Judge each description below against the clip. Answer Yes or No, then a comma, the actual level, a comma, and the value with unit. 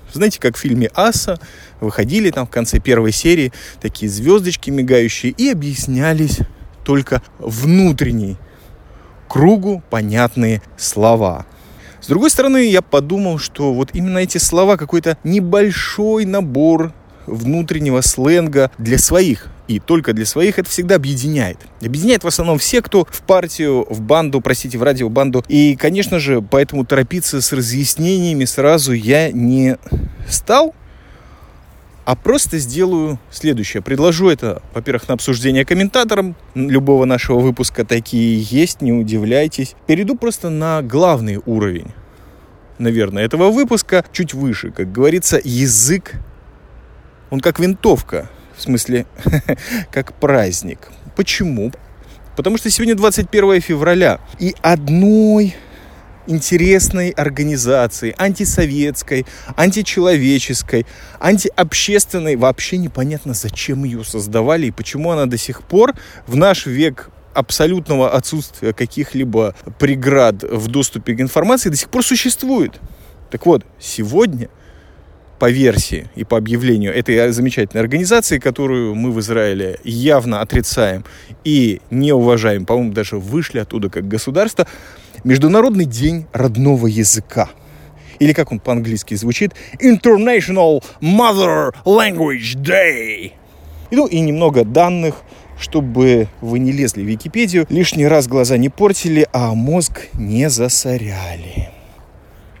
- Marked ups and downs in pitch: Yes, wide, 7.0 semitones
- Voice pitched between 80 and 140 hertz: Yes, low, 135 Hz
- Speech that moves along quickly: No, average, 120 wpm